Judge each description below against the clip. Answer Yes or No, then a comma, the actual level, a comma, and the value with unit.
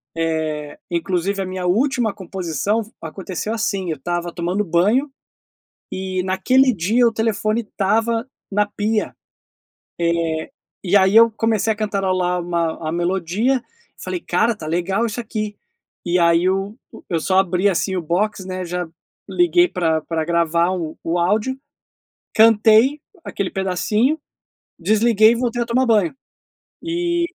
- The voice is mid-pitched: No, high, 195 Hz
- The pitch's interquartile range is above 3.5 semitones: Yes, average, 4.5 semitones